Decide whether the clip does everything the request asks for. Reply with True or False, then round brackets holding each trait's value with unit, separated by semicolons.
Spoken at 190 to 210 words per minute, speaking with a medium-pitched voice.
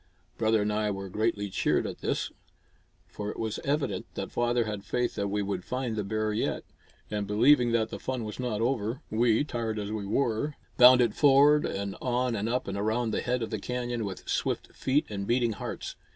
False (205 wpm; 110 Hz)